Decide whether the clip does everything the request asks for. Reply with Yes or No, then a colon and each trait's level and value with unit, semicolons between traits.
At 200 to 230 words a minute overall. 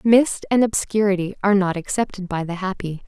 No: average, 175 wpm